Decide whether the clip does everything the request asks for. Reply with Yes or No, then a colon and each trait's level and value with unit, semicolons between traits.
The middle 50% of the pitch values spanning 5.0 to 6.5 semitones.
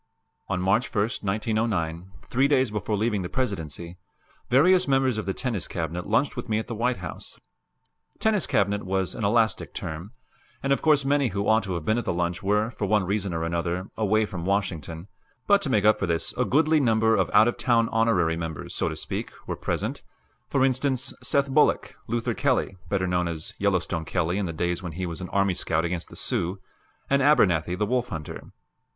Yes: average, 5.3 semitones